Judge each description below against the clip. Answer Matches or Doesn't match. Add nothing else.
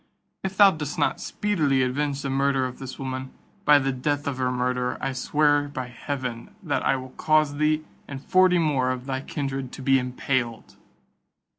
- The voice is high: Doesn't match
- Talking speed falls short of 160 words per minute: Doesn't match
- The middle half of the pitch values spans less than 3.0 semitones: Matches